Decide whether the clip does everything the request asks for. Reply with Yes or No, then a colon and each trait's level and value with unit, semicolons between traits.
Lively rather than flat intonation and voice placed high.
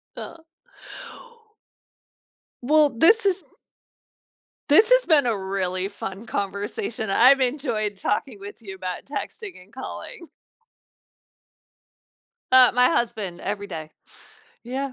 Yes: wide, 6.4 semitones; high, 235 Hz